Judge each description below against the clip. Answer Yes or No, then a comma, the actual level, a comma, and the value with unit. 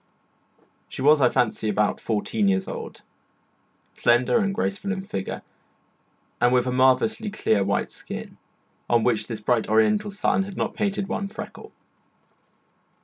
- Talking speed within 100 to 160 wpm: Yes, average, 145 wpm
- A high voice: No, low, 125 Hz